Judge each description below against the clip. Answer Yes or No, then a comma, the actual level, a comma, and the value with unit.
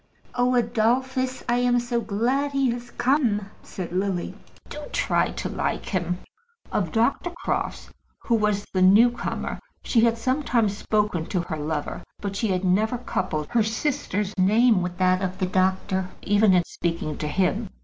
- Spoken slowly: No, average, 165 wpm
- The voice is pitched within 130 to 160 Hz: No, high, 210 Hz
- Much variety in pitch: No, average, 4.5 semitones